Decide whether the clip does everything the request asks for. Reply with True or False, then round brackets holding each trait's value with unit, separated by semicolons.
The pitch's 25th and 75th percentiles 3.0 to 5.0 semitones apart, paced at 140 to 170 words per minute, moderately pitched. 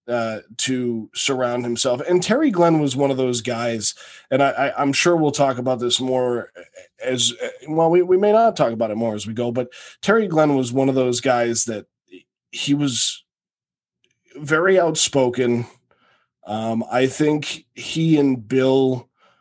False (4.0 semitones; 165 wpm; 130 Hz)